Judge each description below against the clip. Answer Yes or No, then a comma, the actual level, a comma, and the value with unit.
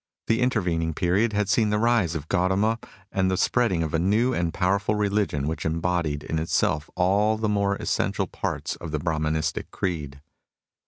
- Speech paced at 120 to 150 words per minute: No, average, 170 wpm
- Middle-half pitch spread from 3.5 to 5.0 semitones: Yes, average, 4.5 semitones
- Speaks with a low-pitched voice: Yes, very low, 95 Hz